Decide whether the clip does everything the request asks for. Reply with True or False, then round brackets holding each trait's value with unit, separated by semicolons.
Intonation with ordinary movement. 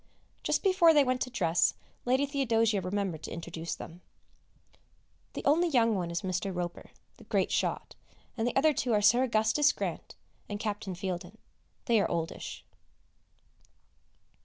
False (6.1 semitones)